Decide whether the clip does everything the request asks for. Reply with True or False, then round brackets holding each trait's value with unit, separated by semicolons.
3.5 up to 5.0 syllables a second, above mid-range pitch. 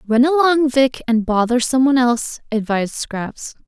True (4.9 syllables/s; 250 Hz)